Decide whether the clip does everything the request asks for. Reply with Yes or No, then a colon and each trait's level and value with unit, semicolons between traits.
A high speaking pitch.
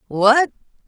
Yes: high, 245 Hz